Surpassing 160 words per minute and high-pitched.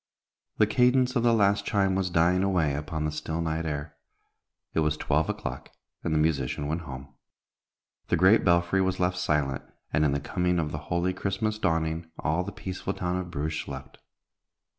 No: average, 185 wpm; very low, 85 Hz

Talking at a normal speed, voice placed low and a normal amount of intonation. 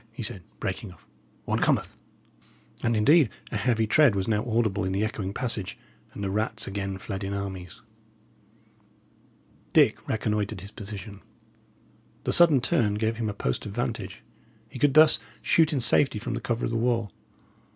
Yes: average, 170 wpm; low, 110 Hz; average, 3.1 semitones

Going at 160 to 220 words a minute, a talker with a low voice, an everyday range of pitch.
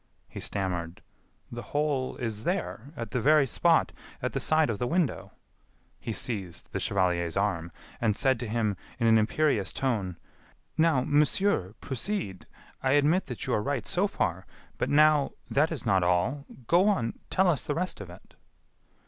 No: average, 175 wpm; low, 125 Hz; wide, 6.9 semitones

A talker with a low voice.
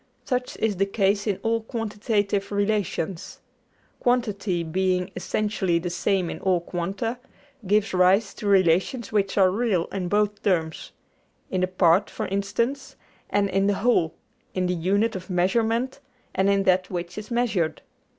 No: high, 195 Hz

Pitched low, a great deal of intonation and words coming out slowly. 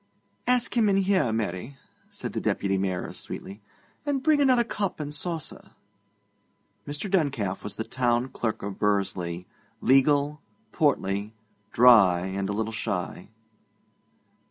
Yes: low, 120 Hz; wide, 8.4 semitones; slow, 130 wpm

